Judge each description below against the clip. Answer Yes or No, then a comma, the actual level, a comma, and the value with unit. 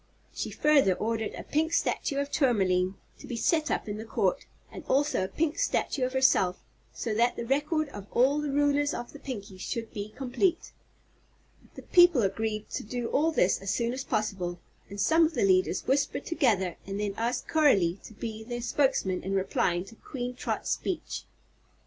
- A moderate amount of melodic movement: No, wide, 6.2 semitones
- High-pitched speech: Yes, high, 240 Hz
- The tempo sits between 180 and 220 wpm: Yes, average, 185 wpm